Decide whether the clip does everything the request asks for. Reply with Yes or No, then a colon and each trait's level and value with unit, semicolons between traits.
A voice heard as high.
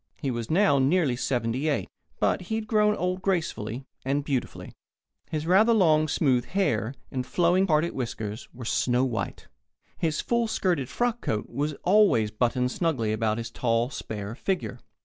No: medium, 140 Hz